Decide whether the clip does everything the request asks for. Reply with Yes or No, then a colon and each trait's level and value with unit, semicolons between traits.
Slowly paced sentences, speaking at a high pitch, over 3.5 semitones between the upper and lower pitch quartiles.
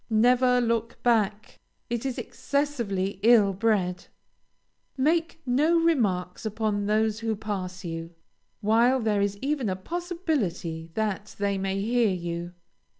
Yes: slow, 125 wpm; high, 215 Hz; average, 4.3 semitones